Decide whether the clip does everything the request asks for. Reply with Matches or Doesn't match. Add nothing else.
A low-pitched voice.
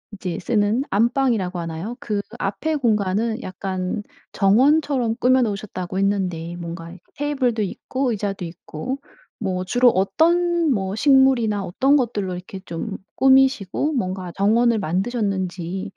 Doesn't match